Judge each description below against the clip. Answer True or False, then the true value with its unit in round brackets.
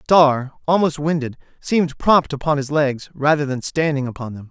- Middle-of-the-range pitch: True (145 Hz)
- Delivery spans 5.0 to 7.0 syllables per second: True (5.2 syllables/s)